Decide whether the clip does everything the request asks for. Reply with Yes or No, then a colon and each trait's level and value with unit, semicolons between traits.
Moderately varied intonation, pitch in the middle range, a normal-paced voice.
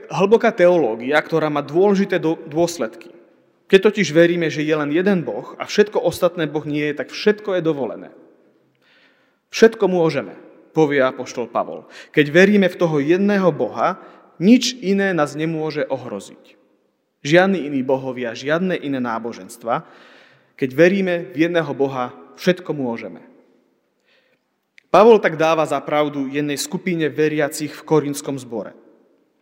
Yes: average, 4.0 semitones; medium, 160 Hz; average, 130 wpm